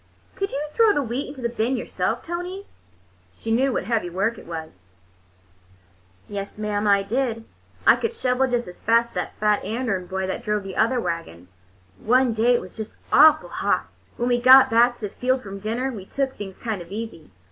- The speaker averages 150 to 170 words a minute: No, average, 200 wpm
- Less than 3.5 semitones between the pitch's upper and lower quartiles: No, average, 4.4 semitones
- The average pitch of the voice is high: Yes, high, 230 Hz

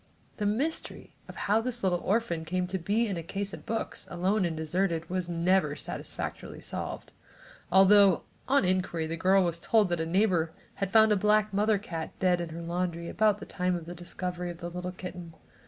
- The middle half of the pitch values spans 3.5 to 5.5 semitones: No, average, 3.1 semitones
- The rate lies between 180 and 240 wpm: Yes, average, 200 wpm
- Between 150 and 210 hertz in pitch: Yes, medium, 185 Hz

